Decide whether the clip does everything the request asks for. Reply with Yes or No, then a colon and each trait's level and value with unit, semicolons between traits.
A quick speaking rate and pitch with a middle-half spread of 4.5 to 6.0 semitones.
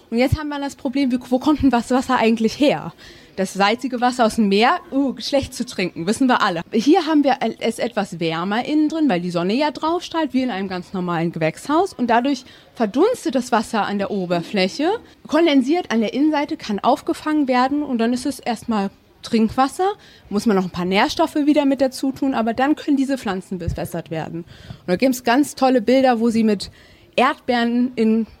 Yes: fast, 205 wpm; wide, 5.4 semitones